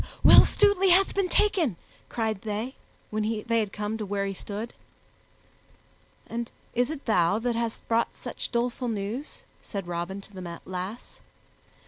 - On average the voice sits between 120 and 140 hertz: No, high, 220 Hz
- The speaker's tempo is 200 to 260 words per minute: No, average, 150 wpm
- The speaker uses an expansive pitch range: No, average, 3.5 semitones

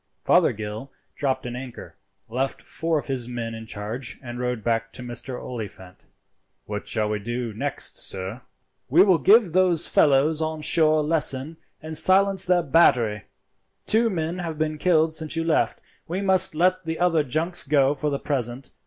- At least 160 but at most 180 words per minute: Yes, average, 170 wpm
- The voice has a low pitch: No, medium, 145 Hz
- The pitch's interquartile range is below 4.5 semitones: No, wide, 5.4 semitones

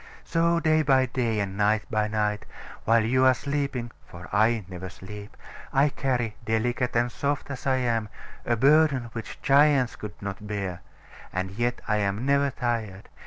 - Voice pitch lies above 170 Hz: No, low, 120 Hz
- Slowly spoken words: No, average, 165 wpm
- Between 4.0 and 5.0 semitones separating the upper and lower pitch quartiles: Yes, average, 4.3 semitones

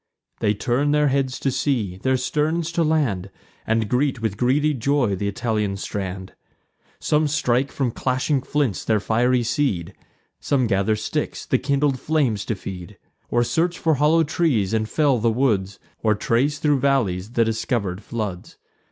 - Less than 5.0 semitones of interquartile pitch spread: No, average, 5.3 semitones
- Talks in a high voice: No, low, 125 Hz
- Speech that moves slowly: No, average, 160 wpm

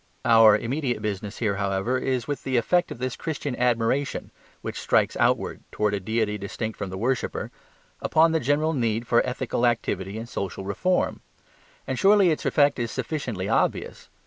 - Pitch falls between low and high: No, low, 120 Hz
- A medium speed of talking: Yes, average, 170 wpm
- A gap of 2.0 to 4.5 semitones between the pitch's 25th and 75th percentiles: No, average, 4.9 semitones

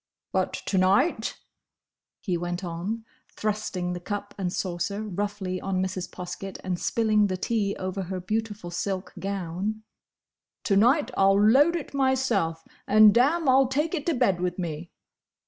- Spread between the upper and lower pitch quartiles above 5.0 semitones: No, average, 3.6 semitones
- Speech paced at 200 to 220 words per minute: No, average, 150 wpm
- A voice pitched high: Yes, high, 200 Hz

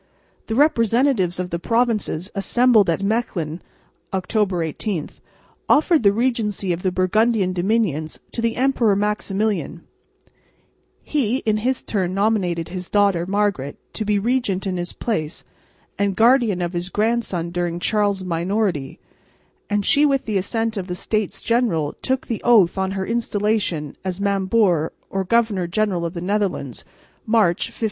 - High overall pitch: Yes, high, 200 Hz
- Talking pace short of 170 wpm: Yes, average, 145 wpm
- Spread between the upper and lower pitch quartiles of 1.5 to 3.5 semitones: No, average, 4.0 semitones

